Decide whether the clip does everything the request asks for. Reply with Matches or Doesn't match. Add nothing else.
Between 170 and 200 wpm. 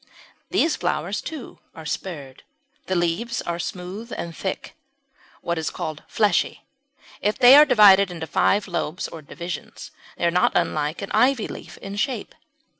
Doesn't match